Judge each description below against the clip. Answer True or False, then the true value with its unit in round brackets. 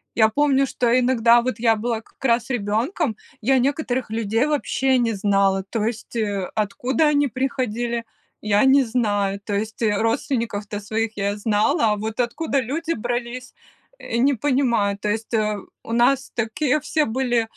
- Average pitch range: True (3.4 semitones)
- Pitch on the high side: True (235 Hz)